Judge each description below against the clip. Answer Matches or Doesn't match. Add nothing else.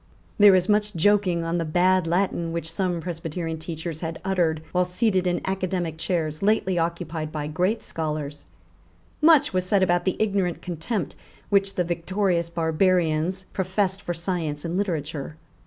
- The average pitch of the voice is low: Doesn't match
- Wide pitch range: Doesn't match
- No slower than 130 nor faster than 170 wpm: Matches